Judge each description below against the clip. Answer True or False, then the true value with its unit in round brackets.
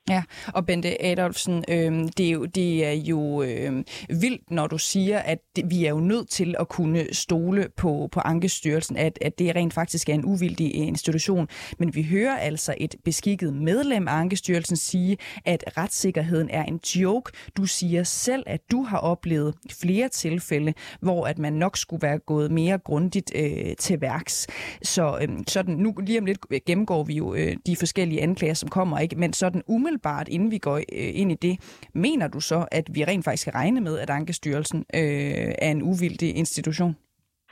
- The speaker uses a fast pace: False (185 wpm)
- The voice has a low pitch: False (170 Hz)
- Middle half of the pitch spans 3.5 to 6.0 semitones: False (3.1 semitones)